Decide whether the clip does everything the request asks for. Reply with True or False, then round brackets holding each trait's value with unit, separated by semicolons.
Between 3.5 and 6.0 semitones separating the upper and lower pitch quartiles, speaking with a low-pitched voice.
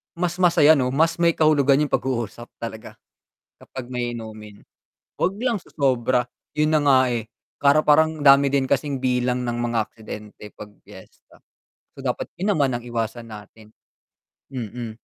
True (3.9 semitones; 130 Hz)